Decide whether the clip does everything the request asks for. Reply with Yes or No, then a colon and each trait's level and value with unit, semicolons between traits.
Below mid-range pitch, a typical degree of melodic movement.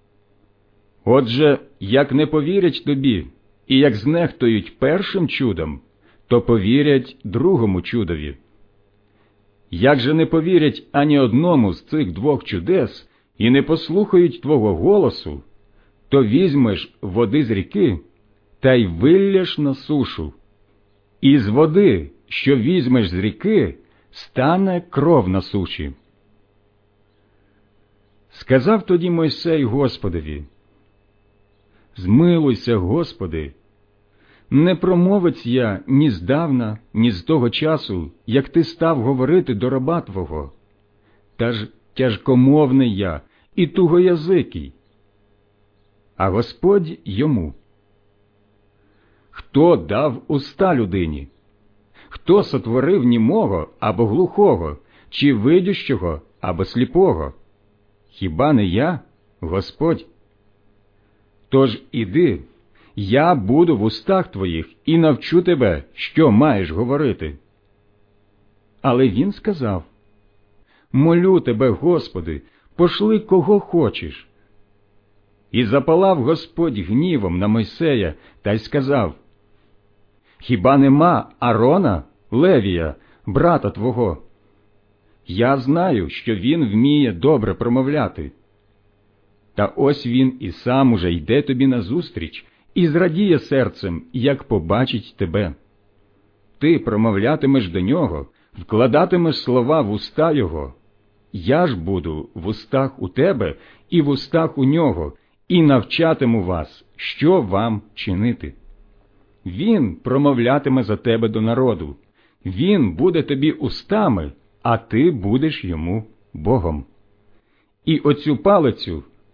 No: low, 110 Hz; wide, 5.8 semitones